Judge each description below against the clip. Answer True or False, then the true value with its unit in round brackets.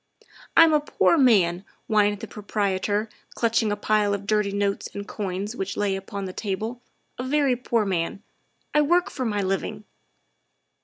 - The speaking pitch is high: True (210 Hz)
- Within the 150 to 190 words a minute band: True (175 wpm)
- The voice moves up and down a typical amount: True (3.0 semitones)